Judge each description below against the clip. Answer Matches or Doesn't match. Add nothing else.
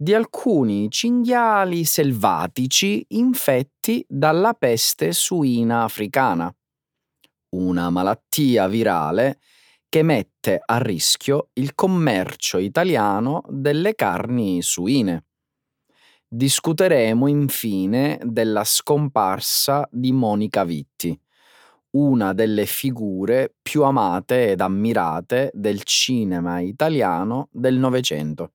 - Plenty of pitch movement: Matches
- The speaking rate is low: Matches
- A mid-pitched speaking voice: Doesn't match